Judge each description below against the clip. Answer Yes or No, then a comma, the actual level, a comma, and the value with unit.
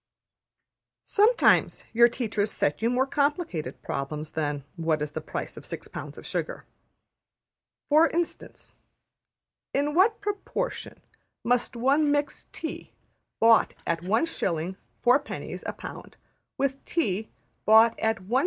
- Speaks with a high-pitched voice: Yes, high, 240 Hz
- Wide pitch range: Yes, wide, 8.1 semitones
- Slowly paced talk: Yes, slow, 125 wpm